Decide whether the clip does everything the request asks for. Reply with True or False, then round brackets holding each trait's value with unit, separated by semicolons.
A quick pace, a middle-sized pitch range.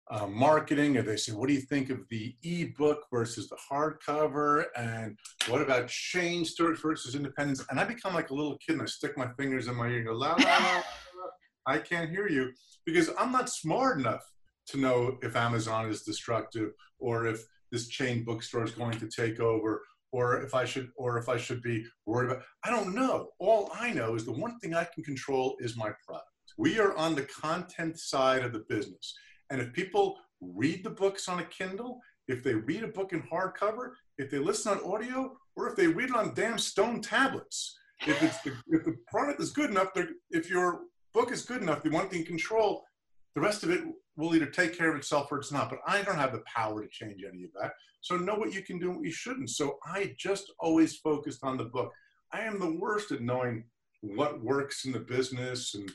False (225 wpm; 7.9 semitones)